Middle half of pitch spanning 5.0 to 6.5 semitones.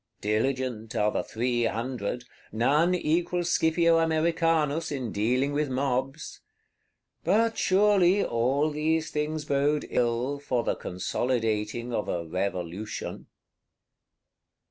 Yes: wide, 5.5 semitones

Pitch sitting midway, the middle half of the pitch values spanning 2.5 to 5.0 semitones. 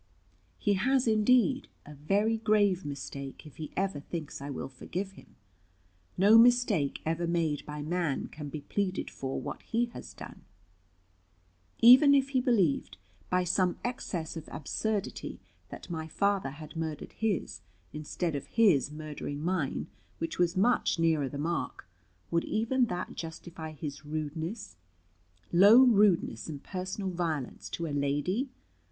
No: medium, 170 Hz; wide, 5.6 semitones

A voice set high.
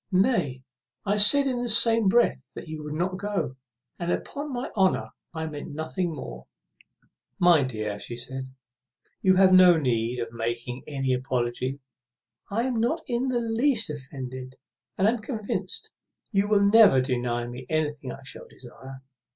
No: medium, 160 Hz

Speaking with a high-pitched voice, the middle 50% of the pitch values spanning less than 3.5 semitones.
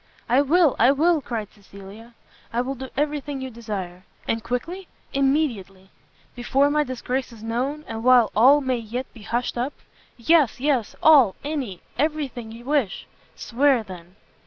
No: very high, 250 Hz; average, 4.1 semitones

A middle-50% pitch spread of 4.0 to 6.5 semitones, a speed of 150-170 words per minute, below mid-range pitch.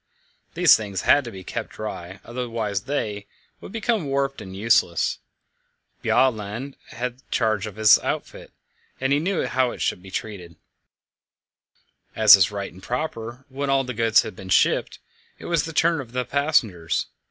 Yes: average, 5.2 semitones; average, 165 wpm; low, 115 Hz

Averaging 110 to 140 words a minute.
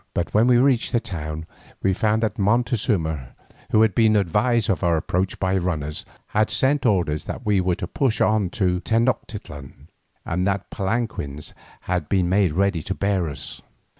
No: average, 170 wpm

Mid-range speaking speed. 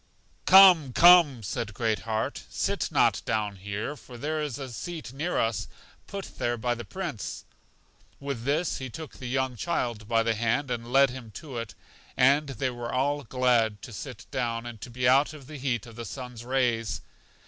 Yes: average, 190 wpm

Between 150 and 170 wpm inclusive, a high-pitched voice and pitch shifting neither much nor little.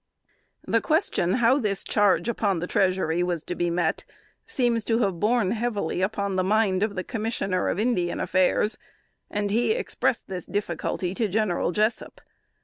Yes: average, 160 wpm; high, 200 Hz; average, 3.7 semitones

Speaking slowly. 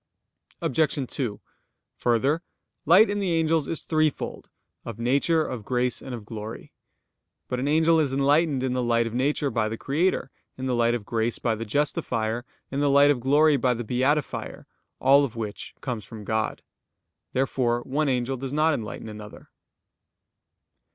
No: average, 165 wpm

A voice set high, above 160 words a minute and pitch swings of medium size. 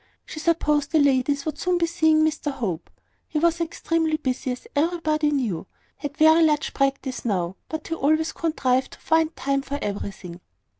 Yes: very high, 300 Hz; average, 170 wpm; average, 3.4 semitones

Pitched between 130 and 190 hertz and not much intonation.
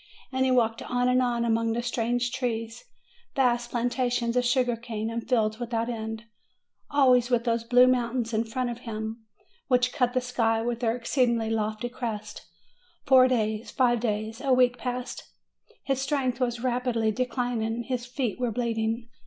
No: high, 240 Hz; narrow, 1.7 semitones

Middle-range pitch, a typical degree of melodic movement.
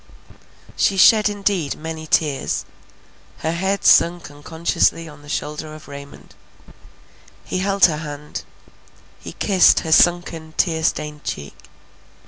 Yes: medium, 160 Hz; average, 3.1 semitones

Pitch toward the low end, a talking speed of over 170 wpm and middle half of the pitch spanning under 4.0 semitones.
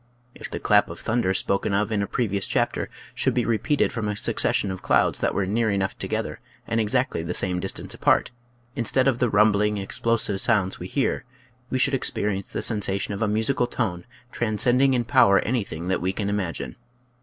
Yes: low, 105 Hz; average, 200 wpm; average, 3.3 semitones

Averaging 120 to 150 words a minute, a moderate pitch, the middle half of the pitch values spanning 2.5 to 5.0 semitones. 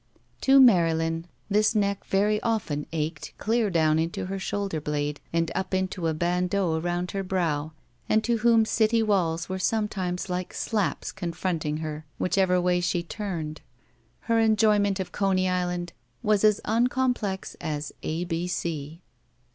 Yes: average, 145 wpm; medium, 180 Hz; average, 4.0 semitones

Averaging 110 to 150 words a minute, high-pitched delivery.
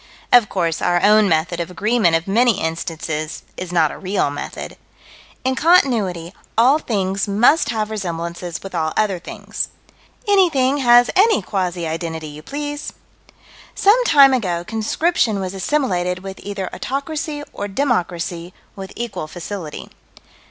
Yes: average, 140 wpm; high, 195 Hz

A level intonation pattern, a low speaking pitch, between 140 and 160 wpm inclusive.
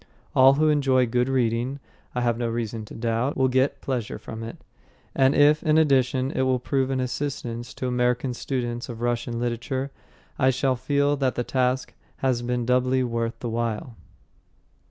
No: narrow, 1.9 semitones; low, 125 Hz; average, 175 wpm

